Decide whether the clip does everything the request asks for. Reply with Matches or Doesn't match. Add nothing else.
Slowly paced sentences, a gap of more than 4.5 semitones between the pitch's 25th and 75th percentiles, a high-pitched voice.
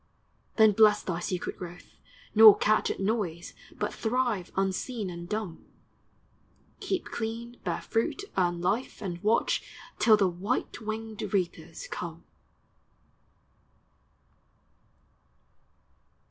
Doesn't match